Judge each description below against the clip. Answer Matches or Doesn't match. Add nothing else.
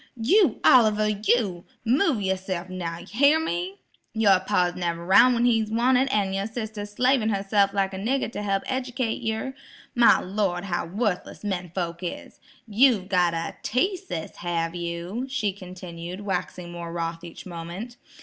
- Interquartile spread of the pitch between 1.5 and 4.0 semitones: Doesn't match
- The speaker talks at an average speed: Matches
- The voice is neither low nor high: Doesn't match